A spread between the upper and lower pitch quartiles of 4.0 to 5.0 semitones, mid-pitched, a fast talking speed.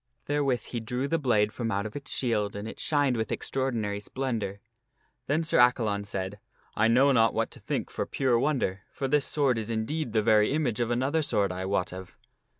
No: average, 4.5 semitones; low, 115 Hz; fast, 230 wpm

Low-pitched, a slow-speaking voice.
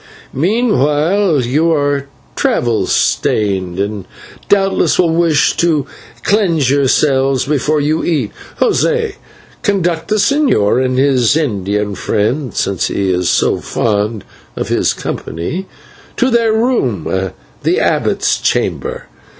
No: medium, 145 Hz; slow, 115 wpm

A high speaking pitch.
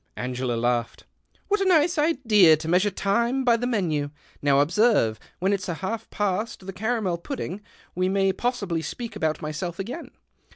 Yes: high, 195 Hz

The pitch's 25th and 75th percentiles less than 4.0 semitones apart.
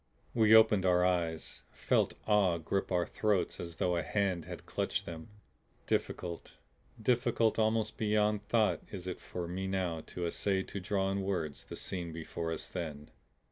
Yes: average, 3.5 semitones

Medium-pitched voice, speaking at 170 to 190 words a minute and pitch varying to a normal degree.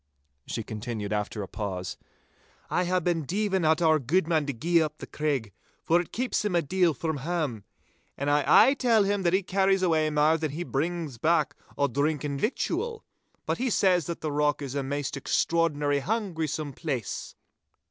Yes: medium, 155 Hz; average, 185 wpm; average, 4.0 semitones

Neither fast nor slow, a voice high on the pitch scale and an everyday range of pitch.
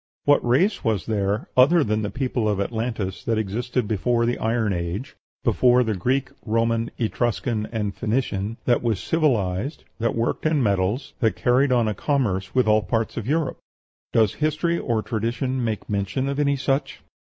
No: average, 170 wpm; low, 115 Hz; average, 3.4 semitones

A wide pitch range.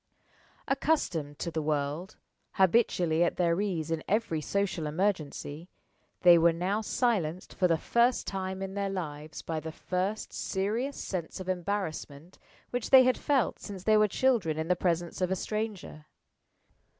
No: average, 4.2 semitones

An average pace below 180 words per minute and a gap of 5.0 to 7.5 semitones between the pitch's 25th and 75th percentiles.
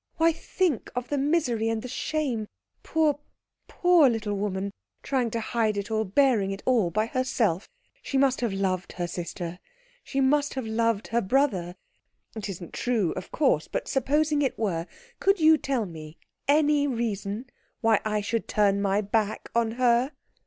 Yes: average, 165 wpm; average, 5.3 semitones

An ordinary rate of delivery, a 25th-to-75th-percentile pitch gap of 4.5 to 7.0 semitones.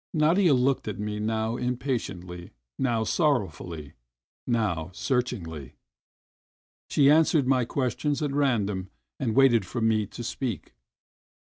No: slow, 115 wpm; average, 4.8 semitones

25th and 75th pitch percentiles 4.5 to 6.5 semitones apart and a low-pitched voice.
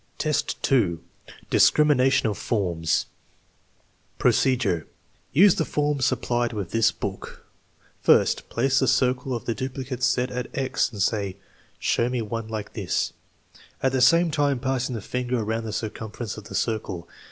No: average, 3.4 semitones; low, 120 Hz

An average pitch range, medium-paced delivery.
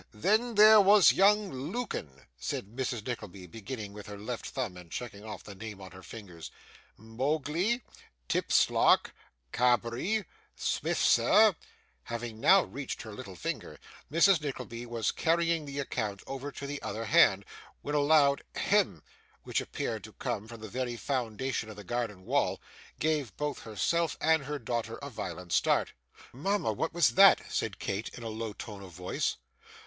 No: wide, 6.6 semitones; average, 160 wpm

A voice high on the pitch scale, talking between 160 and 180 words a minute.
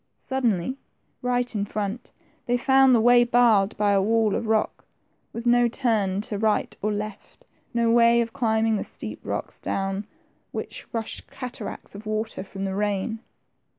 Yes: high, 220 Hz; average, 165 wpm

